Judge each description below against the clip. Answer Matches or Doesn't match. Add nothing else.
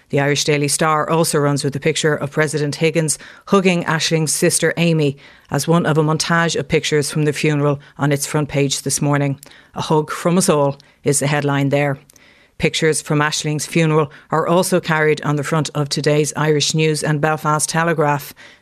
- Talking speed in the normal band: Matches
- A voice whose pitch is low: Doesn't match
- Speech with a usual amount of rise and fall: Doesn't match